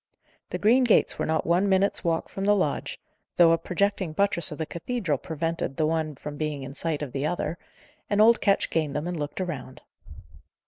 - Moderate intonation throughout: Yes, average, 4.4 semitones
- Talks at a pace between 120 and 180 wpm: No, average, 200 wpm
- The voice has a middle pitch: Yes, medium, 165 Hz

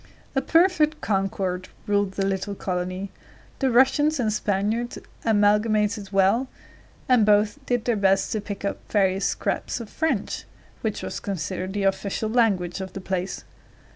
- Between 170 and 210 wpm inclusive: No, average, 145 wpm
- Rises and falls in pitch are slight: No, average, 3.1 semitones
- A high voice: Yes, high, 205 Hz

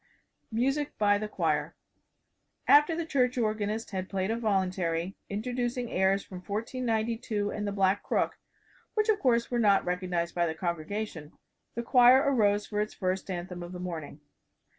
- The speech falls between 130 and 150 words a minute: No, average, 160 wpm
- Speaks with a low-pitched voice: No, high, 205 Hz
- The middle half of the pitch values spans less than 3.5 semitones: No, average, 4.5 semitones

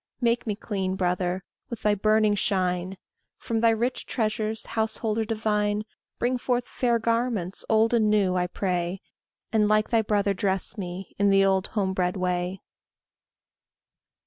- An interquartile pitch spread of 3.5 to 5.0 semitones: No, average, 2.9 semitones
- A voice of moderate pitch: No, high, 210 Hz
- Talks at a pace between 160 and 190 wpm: No, average, 145 wpm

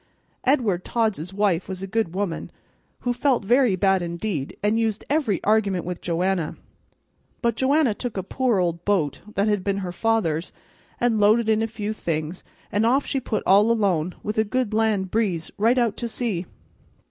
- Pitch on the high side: Yes, high, 210 Hz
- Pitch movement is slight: No, average, 3.7 semitones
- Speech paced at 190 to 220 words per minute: No, average, 180 wpm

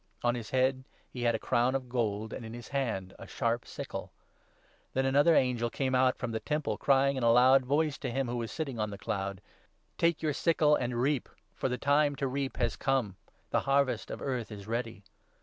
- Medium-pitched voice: No, low, 125 Hz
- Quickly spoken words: Yes, fast, 225 wpm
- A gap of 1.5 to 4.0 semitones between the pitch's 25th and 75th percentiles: Yes, average, 2.9 semitones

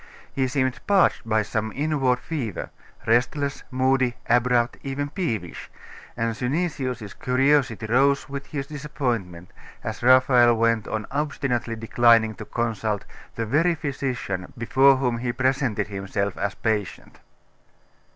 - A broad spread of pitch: No, average, 3.7 semitones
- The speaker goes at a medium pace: No, slow, 120 wpm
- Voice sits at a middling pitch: No, low, 125 Hz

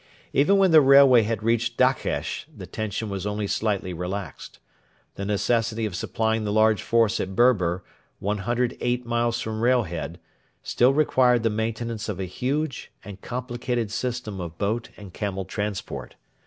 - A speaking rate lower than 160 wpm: Yes, average, 150 wpm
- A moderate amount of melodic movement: Yes, average, 3.2 semitones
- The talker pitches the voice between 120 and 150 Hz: No, low, 110 Hz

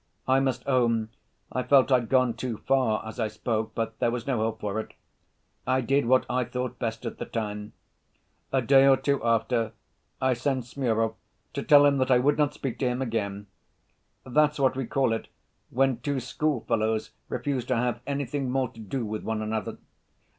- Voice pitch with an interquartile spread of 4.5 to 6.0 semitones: No, average, 3.0 semitones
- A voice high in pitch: No, low, 125 Hz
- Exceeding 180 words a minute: Yes, average, 190 wpm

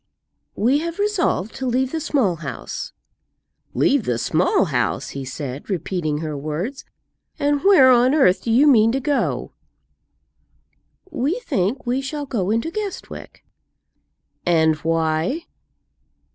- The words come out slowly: Yes, slow, 130 wpm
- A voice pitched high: Yes, high, 235 Hz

